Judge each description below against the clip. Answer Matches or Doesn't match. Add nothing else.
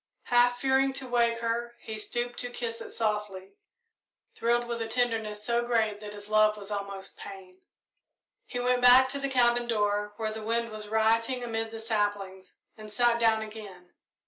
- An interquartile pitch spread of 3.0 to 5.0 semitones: Doesn't match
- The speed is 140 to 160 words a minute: Doesn't match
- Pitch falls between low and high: Doesn't match